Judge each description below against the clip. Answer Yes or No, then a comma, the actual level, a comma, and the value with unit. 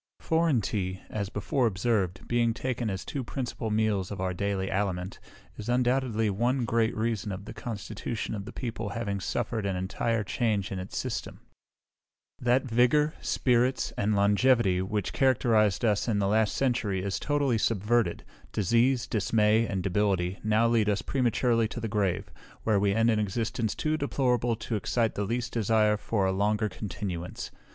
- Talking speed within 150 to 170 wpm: Yes, average, 165 wpm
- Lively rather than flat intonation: No, average, 3.2 semitones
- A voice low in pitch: Yes, low, 110 Hz